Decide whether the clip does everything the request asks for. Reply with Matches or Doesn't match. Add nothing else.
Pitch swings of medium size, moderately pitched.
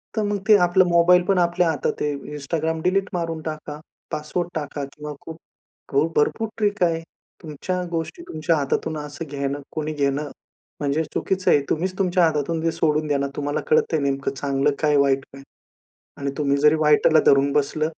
Matches